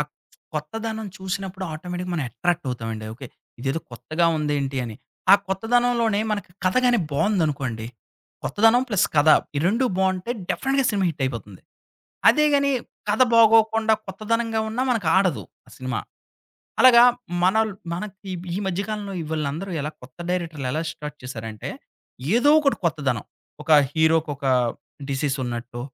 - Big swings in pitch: Yes, wide, 7.7 semitones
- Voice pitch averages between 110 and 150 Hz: No, medium, 180 Hz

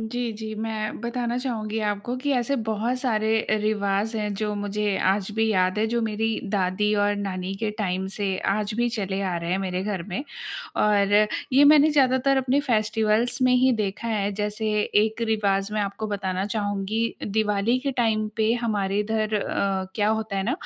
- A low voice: No, high, 215 Hz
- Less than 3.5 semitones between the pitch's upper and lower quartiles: Yes, narrow, 2.4 semitones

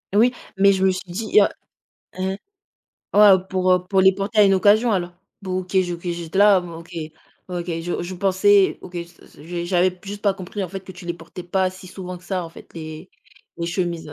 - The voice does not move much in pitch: Yes, narrow, 1.9 semitones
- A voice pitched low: No, medium, 185 Hz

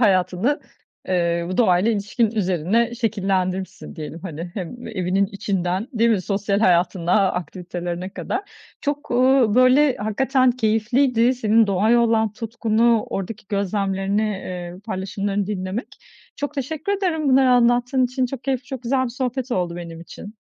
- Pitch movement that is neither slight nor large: Yes, average, 4.9 semitones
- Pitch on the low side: No, high, 215 Hz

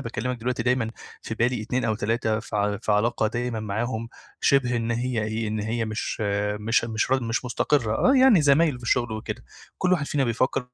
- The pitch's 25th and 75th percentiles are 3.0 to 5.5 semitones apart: No, narrow, 2.4 semitones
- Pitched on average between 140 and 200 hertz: No, low, 115 Hz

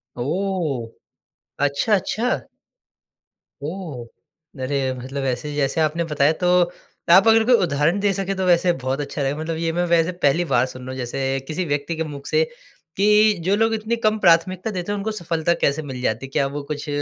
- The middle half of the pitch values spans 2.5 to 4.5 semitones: No, wide, 5.4 semitones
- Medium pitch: Yes, medium, 160 Hz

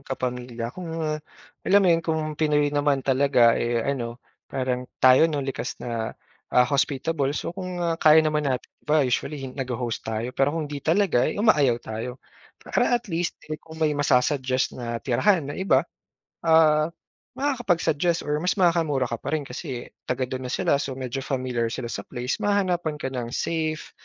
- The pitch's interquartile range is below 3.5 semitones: No, average, 4.2 semitones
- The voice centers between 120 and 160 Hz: Yes, medium, 140 Hz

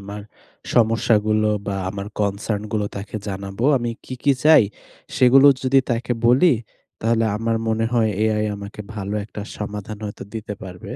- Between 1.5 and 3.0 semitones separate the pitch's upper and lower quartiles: Yes, narrow, 2.4 semitones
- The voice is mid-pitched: No, low, 110 Hz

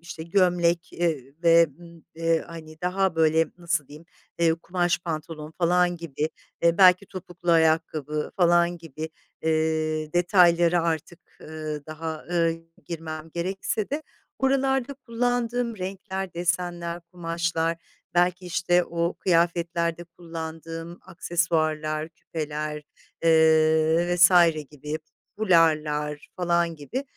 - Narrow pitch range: Yes, narrow, 1.8 semitones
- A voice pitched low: No, medium, 170 Hz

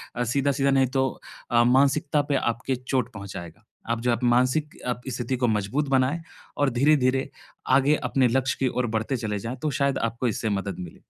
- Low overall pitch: Yes, low, 125 Hz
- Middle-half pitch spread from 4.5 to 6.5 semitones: No, average, 2.8 semitones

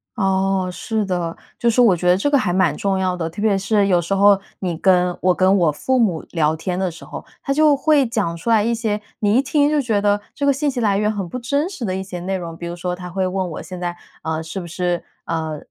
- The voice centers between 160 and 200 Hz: Yes, high, 190 Hz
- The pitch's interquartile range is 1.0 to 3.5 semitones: No, average, 4.0 semitones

